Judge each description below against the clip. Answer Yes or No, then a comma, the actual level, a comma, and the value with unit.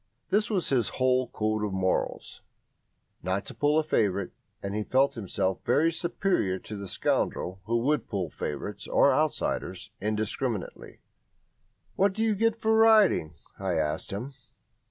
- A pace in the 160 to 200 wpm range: No, average, 150 wpm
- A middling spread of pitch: No, wide, 8.3 semitones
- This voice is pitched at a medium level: No, low, 115 Hz